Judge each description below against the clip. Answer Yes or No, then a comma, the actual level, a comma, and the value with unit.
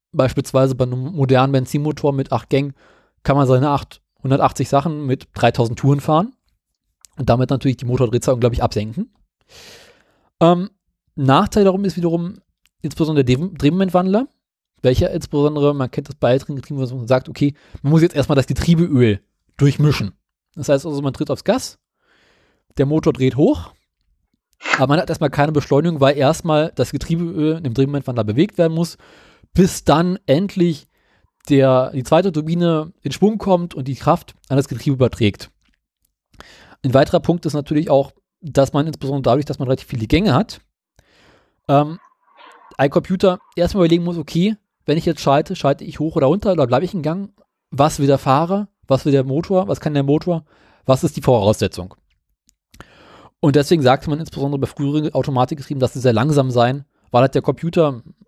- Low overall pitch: No, medium, 145 Hz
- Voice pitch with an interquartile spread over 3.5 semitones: Yes, average, 4.0 semitones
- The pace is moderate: Yes, average, 165 wpm